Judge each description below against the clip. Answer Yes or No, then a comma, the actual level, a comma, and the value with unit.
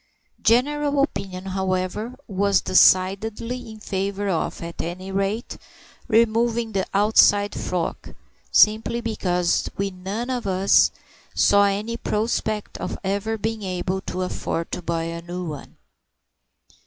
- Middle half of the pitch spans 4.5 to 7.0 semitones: No, average, 3.2 semitones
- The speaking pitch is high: Yes, high, 200 Hz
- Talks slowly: Yes, slow, 125 wpm